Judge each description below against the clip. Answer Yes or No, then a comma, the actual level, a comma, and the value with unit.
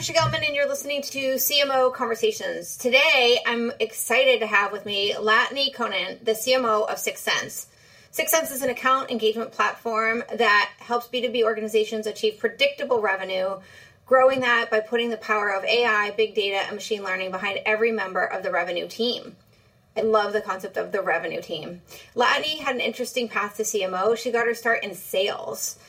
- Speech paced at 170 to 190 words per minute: Yes, average, 175 wpm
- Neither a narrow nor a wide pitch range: Yes, average, 3.1 semitones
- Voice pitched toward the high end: Yes, high, 230 Hz